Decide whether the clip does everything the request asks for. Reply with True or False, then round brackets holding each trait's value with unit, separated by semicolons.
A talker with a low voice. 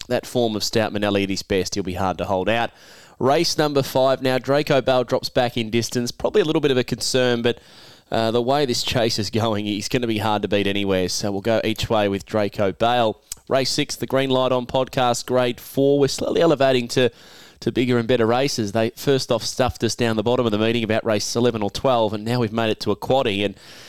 True (120 Hz)